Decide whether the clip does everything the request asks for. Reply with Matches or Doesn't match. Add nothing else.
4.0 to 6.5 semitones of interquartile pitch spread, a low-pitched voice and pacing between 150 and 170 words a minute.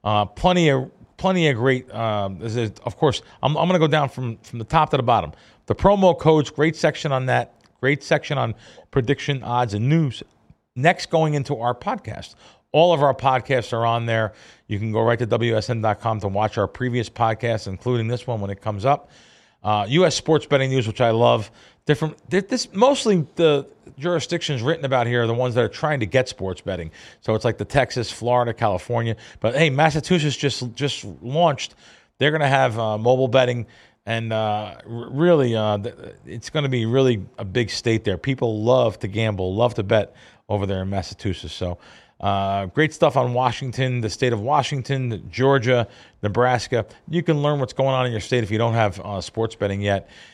Doesn't match